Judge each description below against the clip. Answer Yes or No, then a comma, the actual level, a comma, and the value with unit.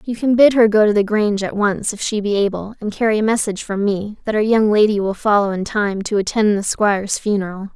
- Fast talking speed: Yes, fast, 255 wpm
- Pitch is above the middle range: Yes, high, 210 Hz